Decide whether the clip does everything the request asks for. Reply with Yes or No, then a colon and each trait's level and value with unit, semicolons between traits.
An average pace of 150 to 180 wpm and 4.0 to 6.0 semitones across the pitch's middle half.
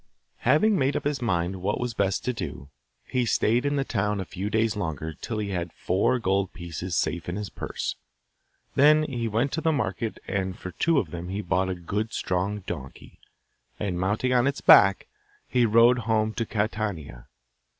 No: average, 190 wpm; average, 4.8 semitones